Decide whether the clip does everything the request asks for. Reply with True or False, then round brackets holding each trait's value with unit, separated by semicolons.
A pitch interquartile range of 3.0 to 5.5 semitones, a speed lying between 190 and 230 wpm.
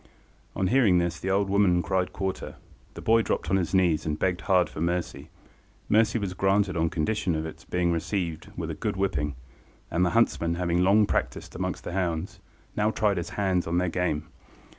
False (2.6 semitones; 195 wpm)